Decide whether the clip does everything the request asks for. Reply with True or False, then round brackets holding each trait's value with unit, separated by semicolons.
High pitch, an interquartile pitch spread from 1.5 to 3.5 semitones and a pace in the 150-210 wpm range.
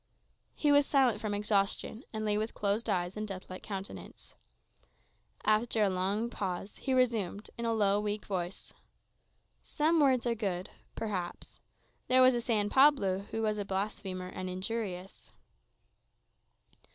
False (210 Hz; 3.2 semitones; 140 wpm)